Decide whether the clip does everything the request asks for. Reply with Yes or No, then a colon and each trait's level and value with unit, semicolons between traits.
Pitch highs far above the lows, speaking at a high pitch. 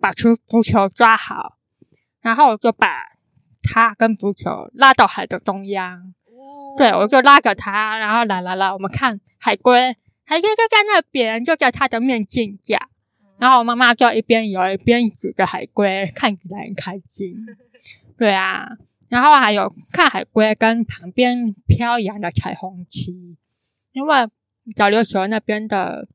No: average, 4.0 semitones; high, 225 Hz